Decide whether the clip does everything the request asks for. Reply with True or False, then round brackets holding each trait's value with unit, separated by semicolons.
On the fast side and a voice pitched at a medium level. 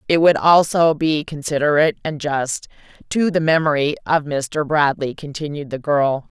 False (150 wpm; 150 Hz)